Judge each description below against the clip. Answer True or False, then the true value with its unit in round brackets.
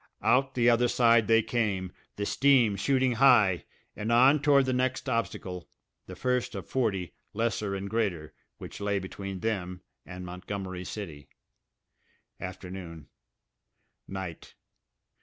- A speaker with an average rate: False (125 wpm)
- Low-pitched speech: True (105 Hz)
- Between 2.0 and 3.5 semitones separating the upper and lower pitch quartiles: False (4.9 semitones)